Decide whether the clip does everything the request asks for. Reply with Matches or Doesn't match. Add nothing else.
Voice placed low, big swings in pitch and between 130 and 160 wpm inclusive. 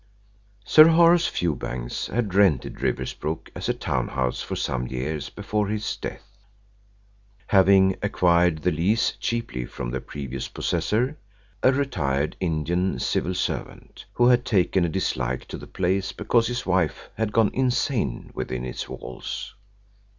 Matches